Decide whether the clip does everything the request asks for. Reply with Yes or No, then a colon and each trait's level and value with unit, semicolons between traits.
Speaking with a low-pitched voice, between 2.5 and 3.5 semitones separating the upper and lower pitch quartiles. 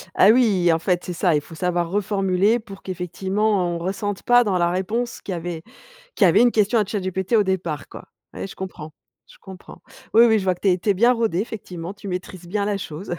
No: high, 190 Hz; average, 2.9 semitones